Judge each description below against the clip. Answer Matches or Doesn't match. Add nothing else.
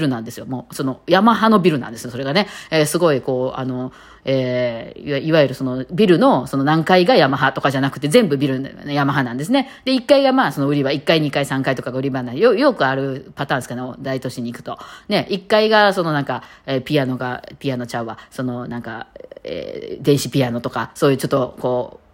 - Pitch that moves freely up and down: Doesn't match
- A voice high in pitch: Doesn't match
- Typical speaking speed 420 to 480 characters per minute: Matches